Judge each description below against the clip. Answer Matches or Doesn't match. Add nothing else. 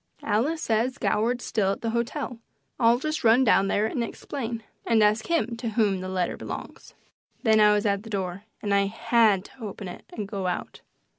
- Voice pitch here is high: Matches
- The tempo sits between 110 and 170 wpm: Doesn't match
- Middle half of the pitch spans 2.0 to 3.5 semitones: Matches